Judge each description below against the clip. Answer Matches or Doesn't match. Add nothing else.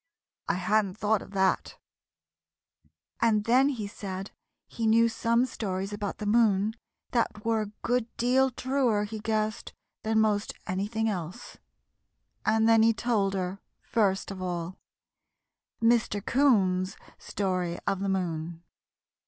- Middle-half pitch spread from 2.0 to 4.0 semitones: Matches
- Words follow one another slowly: Matches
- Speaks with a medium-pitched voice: Doesn't match